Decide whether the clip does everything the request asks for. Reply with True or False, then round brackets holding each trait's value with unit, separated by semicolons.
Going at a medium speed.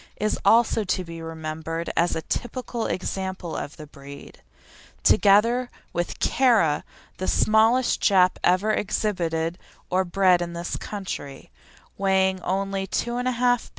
False (130 wpm)